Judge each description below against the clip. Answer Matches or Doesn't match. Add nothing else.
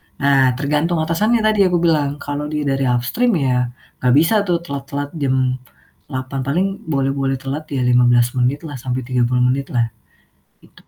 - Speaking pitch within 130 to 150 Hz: Matches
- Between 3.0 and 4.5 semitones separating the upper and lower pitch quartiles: Matches